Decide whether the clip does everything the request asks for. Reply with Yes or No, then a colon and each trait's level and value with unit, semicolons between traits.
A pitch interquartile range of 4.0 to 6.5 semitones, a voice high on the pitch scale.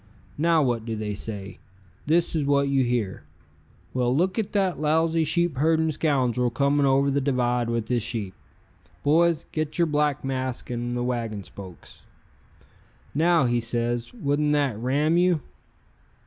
No: average, 4.6 semitones; medium, 140 Hz